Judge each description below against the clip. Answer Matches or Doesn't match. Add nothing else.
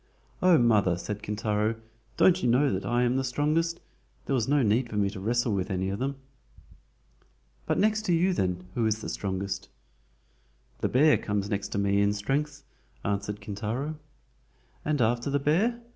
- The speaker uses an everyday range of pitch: Doesn't match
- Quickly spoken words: Doesn't match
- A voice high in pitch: Doesn't match